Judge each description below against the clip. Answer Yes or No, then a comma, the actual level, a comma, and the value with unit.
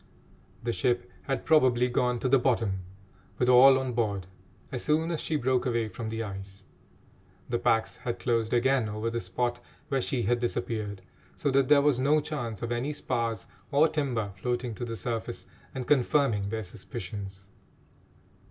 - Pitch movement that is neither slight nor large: Yes, average, 3.0 semitones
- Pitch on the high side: No, low, 120 Hz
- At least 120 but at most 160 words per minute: No, average, 170 wpm